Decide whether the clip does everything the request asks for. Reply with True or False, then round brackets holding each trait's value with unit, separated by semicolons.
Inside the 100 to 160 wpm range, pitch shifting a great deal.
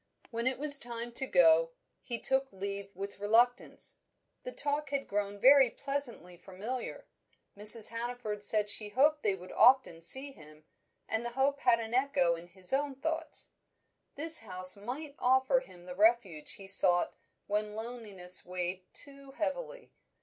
True (155 wpm; 5.8 semitones)